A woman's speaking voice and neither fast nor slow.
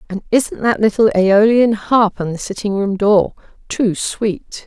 Yes: female; average, 165 wpm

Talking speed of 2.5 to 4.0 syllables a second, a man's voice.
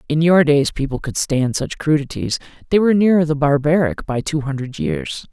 No: 5.2 syllables/s; male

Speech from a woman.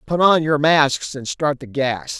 No: male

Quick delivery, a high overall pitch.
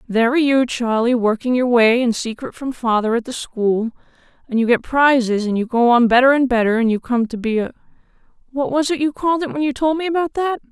Yes: fast, 235 wpm; very high, 250 Hz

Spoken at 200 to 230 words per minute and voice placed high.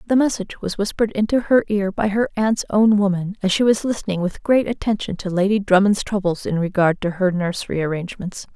Yes: fast, 205 wpm; high, 200 Hz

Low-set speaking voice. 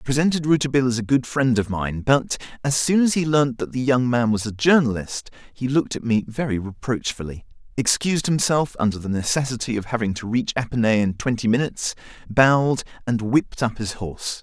Yes: low, 125 Hz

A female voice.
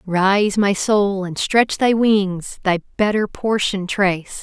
Yes: female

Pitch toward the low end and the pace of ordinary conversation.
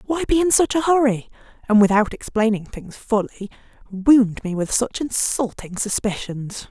No: high, 230 Hz; average, 150 wpm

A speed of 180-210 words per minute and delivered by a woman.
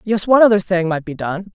No: fast, 270 wpm; female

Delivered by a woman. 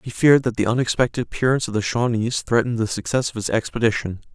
No: male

